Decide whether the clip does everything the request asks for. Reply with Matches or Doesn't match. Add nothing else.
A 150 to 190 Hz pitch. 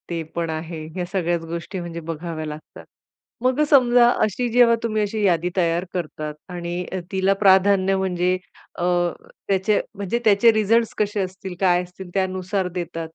Matches